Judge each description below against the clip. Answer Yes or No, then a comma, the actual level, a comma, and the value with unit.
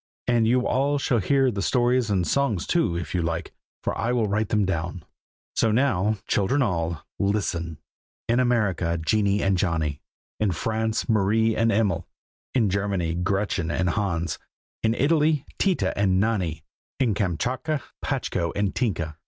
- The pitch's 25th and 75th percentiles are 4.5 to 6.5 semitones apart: Yes, average, 5.1 semitones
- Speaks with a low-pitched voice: Yes, low, 105 Hz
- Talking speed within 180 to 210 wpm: No, average, 155 wpm